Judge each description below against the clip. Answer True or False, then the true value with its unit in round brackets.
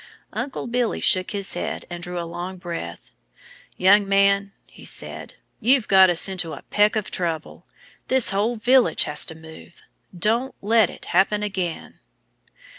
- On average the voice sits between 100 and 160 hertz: False (195 Hz)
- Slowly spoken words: False (155 wpm)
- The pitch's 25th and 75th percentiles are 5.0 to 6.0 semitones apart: False (3.6 semitones)